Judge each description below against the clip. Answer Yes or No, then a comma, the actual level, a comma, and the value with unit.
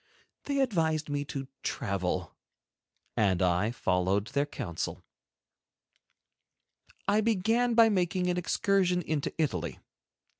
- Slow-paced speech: Yes, slow, 110 wpm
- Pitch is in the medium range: Yes, medium, 155 Hz